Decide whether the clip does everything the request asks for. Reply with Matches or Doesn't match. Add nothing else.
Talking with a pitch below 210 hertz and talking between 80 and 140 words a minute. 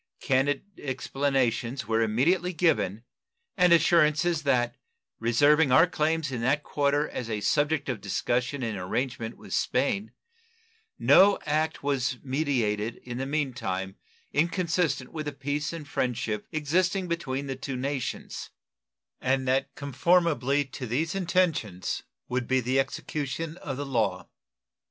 Matches